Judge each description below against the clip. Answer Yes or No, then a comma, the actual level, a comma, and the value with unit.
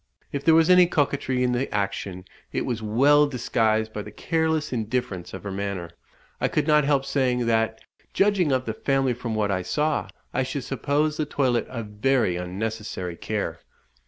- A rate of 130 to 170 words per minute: No, average, 180 wpm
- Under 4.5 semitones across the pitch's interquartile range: No, average, 5.1 semitones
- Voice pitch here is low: Yes, low, 125 Hz